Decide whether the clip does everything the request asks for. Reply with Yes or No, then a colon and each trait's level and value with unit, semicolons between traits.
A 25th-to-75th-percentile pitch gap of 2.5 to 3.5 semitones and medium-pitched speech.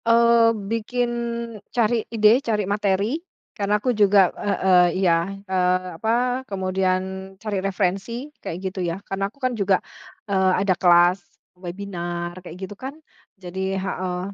No: average, 2.9 semitones; high, 195 Hz